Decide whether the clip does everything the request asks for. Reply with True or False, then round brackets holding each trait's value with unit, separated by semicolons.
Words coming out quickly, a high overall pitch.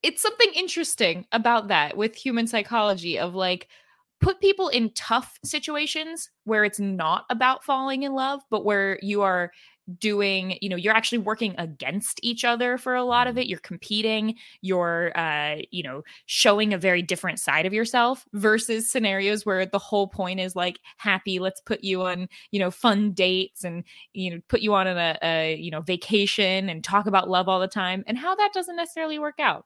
False (190 wpm; 205 Hz)